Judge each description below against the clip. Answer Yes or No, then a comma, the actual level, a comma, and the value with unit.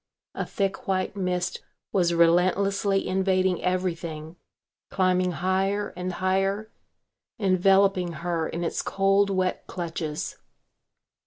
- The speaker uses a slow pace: Yes, slow, 100 wpm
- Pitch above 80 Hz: Yes, medium, 185 Hz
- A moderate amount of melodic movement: No, narrow, 1.8 semitones